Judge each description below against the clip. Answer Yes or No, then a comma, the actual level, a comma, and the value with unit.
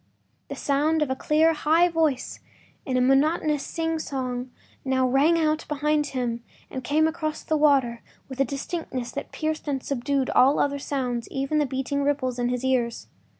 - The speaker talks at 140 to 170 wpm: No, average, 180 wpm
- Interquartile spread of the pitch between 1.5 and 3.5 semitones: Yes, average, 2.9 semitones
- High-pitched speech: Yes, very high, 280 Hz